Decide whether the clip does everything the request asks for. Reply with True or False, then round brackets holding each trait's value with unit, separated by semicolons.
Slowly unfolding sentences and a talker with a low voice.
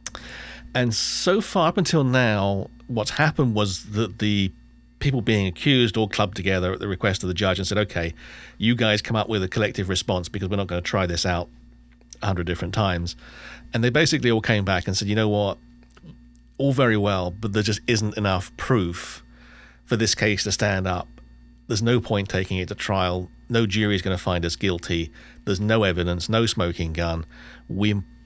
False (195 wpm; 100 Hz)